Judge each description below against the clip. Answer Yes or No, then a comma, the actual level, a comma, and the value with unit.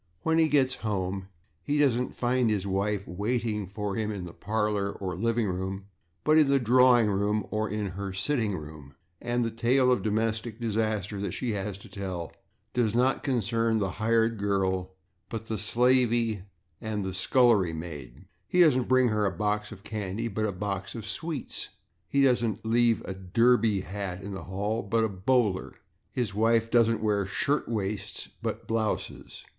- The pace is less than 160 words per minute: No, average, 170 wpm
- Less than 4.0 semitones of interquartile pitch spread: Yes, average, 3.2 semitones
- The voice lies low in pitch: Yes, low, 110 Hz